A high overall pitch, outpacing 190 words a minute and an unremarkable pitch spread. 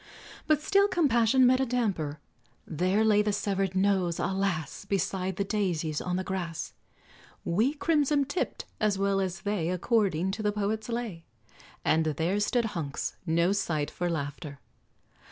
No: high, 195 Hz; average, 150 wpm; average, 4.4 semitones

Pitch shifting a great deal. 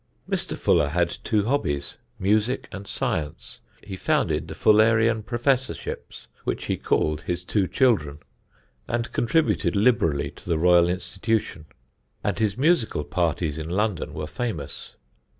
Yes: wide, 5.7 semitones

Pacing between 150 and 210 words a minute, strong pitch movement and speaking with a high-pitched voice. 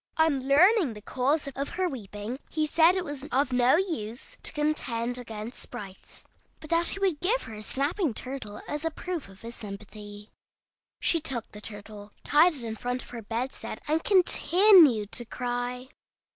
Yes: average, 175 wpm; wide, 6.1 semitones; very high, 260 Hz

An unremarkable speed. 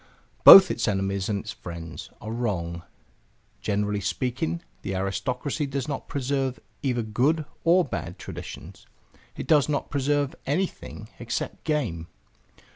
No: slow, 125 wpm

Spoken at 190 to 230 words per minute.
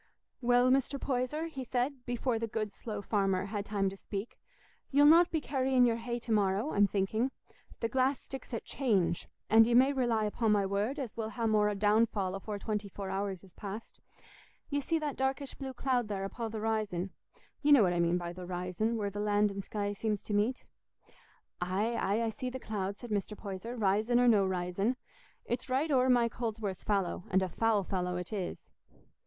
Yes: average, 200 wpm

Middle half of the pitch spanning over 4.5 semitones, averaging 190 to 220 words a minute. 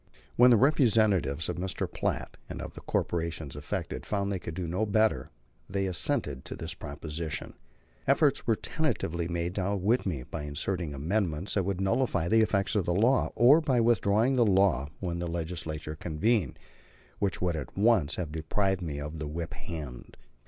No: average, 5.2 semitones; average, 175 wpm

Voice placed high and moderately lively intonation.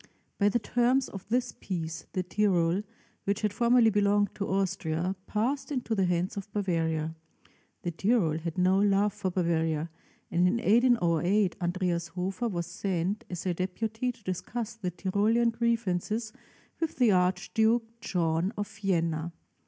Yes: high, 195 Hz; average, 4.1 semitones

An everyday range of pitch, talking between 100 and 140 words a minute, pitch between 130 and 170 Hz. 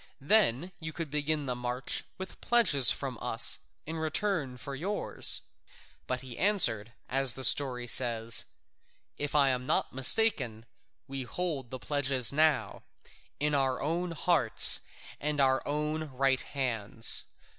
Yes: average, 3.8 semitones; slow, 135 wpm; medium, 140 Hz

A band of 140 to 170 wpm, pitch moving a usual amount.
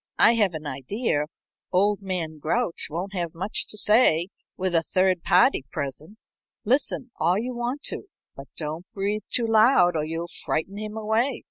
Yes: average, 165 wpm; average, 5.0 semitones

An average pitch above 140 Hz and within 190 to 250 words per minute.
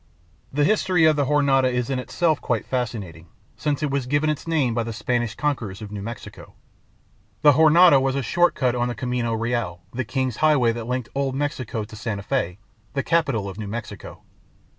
No: low, 125 Hz; average, 195 wpm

